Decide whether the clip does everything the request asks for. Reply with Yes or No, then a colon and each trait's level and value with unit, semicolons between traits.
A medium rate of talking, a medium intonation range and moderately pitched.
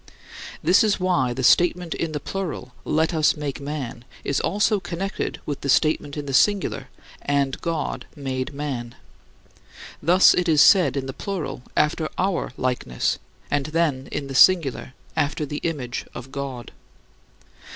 Yes: average, 150 wpm; average, 4.1 semitones; medium, 150 Hz